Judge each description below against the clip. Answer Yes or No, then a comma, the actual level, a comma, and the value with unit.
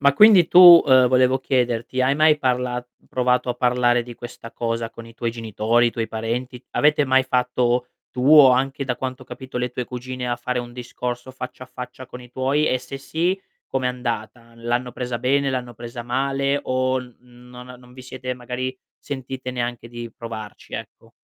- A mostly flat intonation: Yes, narrow, 1.3 semitones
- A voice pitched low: Yes, low, 125 Hz